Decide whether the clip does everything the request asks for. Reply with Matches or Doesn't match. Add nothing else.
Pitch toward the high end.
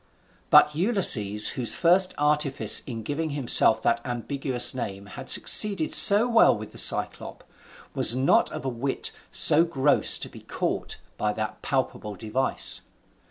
Doesn't match